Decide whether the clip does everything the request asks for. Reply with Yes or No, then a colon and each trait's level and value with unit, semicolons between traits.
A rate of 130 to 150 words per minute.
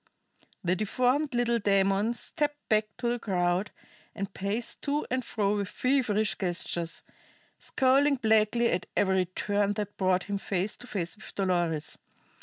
Yes: average, 145 wpm